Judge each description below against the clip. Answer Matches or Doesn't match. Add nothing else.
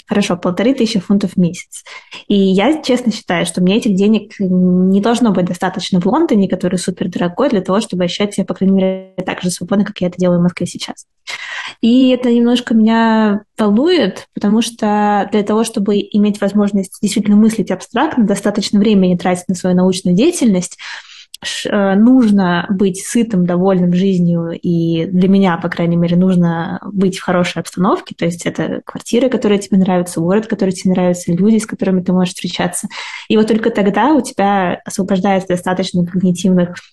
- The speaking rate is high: Matches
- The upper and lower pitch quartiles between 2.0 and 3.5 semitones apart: Matches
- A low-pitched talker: Doesn't match